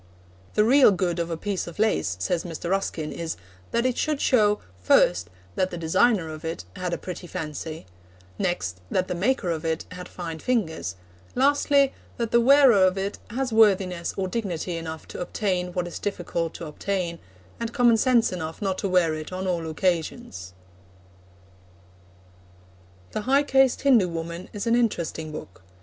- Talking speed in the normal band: Yes, average, 170 wpm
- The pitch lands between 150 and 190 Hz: Yes, medium, 185 Hz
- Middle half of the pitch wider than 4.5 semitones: Yes, average, 5.2 semitones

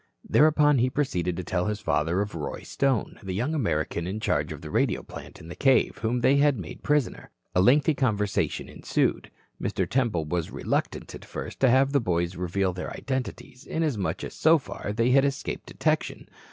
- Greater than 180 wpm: Yes, average, 190 wpm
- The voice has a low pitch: Yes, low, 115 Hz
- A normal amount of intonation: No, wide, 7.1 semitones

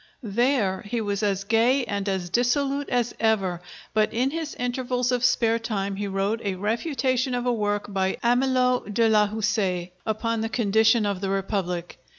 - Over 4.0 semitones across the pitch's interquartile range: No, average, 3.7 semitones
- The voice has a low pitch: No, high, 220 Hz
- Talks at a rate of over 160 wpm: Yes, average, 170 wpm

